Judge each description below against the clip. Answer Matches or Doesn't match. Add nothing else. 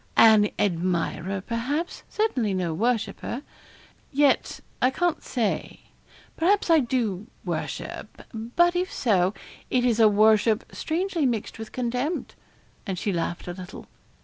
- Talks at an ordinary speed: Doesn't match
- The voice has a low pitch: Doesn't match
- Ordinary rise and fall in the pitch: Doesn't match